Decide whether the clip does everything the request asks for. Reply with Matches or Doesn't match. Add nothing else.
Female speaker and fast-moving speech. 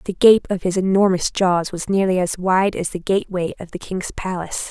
Matches